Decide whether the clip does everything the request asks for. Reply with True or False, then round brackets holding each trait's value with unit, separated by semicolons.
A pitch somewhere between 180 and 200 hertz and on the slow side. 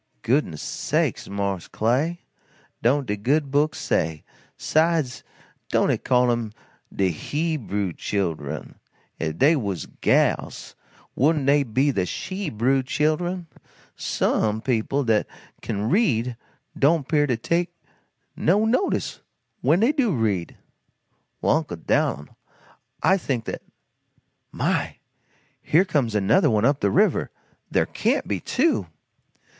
False (135 Hz; 125 wpm)